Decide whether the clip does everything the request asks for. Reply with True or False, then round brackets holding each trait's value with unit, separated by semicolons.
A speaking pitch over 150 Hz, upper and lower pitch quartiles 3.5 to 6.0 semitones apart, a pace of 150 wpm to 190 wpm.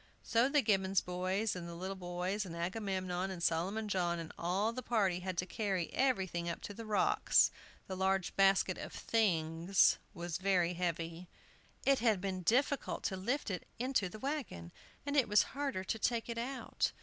True (190 Hz; 4.1 semitones; 180 wpm)